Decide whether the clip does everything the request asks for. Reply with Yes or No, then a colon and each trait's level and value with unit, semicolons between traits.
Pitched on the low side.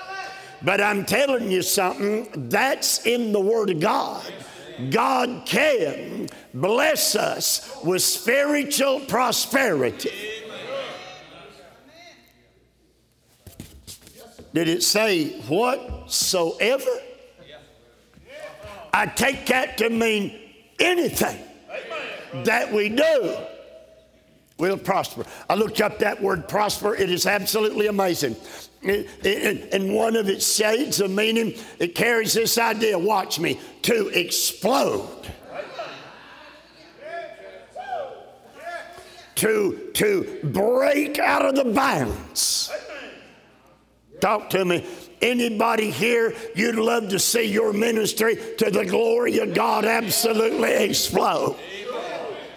No: high, 225 Hz